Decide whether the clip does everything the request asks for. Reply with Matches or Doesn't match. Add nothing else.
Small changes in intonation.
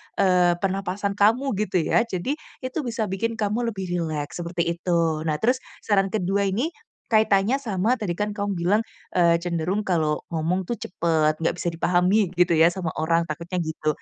Doesn't match